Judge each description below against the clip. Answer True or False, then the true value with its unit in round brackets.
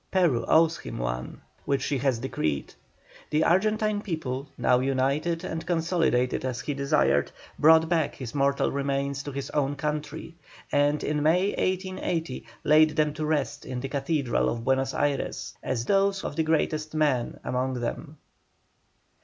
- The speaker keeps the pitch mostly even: False (3.5 semitones)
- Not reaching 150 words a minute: False (155 wpm)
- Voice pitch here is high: False (145 Hz)